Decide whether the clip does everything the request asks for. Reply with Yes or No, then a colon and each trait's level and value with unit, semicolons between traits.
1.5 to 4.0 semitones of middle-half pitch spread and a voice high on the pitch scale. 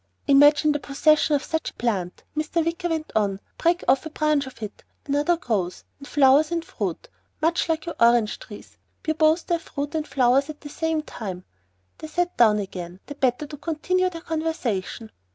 No: average, 4.9 semitones; very high, 295 Hz